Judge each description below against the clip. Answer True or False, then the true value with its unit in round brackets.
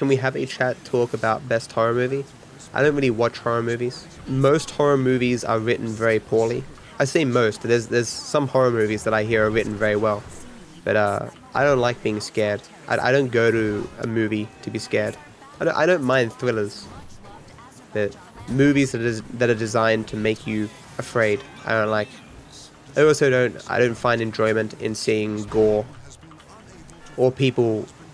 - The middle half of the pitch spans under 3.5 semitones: True (2.8 semitones)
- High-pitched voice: False (115 Hz)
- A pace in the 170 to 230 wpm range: True (190 wpm)